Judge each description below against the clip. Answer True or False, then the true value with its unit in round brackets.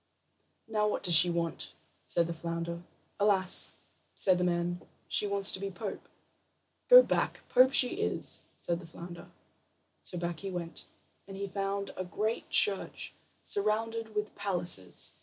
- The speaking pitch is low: False (190 Hz)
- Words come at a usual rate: True (150 wpm)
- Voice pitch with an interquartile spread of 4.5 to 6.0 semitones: False (3.4 semitones)